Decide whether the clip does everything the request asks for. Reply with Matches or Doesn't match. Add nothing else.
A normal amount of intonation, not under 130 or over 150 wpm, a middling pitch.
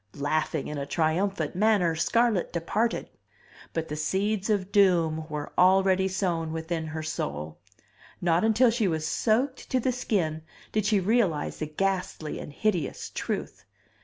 Matches